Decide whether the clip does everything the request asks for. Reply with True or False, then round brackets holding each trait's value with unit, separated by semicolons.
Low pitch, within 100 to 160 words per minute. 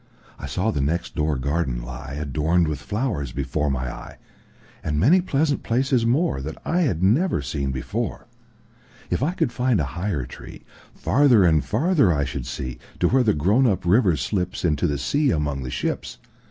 True (85 Hz; 155 wpm)